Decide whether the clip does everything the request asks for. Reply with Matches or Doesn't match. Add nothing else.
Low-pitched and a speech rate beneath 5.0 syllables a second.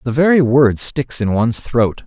Matches